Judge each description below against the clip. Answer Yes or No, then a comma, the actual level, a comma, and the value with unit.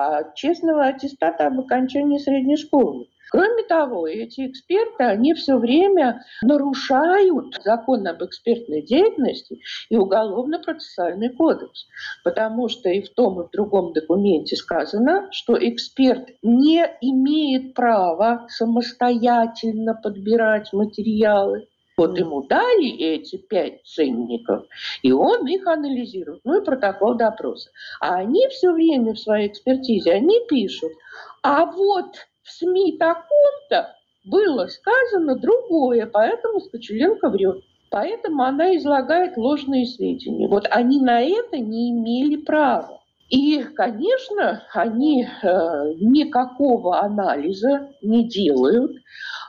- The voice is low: No, very high, 255 Hz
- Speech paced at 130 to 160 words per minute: No, average, 115 wpm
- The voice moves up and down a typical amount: No, wide, 6.4 semitones